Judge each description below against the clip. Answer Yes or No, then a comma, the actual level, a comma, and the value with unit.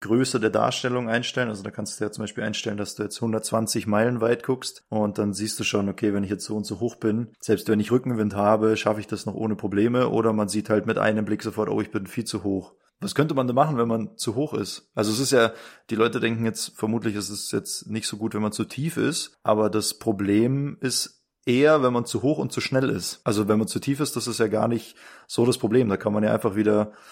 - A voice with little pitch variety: Yes, narrow, 2.3 semitones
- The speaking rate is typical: No, fast, 270 wpm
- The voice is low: Yes, low, 110 Hz